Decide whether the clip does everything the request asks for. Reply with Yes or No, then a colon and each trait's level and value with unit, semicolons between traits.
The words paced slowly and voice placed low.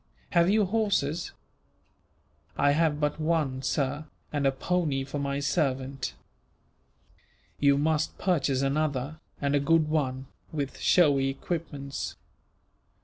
No: slow, 115 wpm; medium, 145 Hz